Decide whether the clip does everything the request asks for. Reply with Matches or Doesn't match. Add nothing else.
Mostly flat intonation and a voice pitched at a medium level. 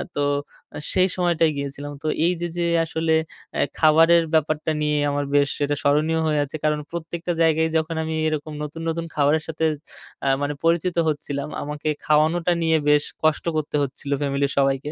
Matches